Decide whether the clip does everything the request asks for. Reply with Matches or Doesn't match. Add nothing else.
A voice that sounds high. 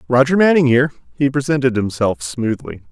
Doesn't match